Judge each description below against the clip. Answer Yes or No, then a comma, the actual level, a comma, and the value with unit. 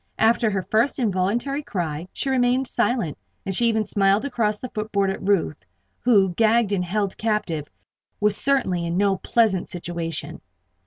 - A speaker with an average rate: Yes, average, 155 wpm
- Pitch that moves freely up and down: No, average, 4.1 semitones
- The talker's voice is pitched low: No, high, 205 Hz